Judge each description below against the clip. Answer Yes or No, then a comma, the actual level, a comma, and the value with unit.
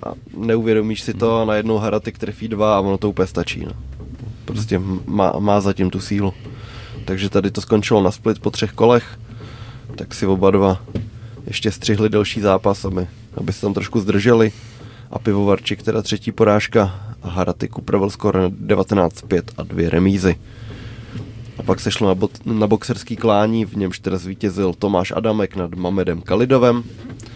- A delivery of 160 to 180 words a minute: Yes, average, 165 wpm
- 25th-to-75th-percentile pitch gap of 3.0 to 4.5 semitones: No, narrow, 2.6 semitones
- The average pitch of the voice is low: Yes, low, 105 Hz